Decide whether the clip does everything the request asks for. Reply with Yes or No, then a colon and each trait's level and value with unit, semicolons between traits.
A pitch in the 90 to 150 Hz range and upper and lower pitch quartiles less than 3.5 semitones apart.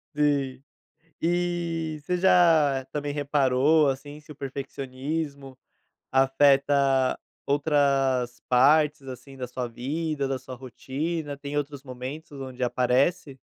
Yes: medium, 140 Hz; narrow, 2.4 semitones